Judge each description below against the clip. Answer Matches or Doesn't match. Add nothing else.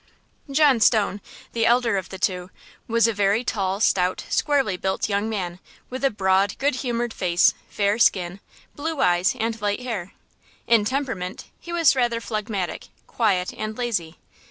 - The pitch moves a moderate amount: Matches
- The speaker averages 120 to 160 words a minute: Matches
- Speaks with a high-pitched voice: Matches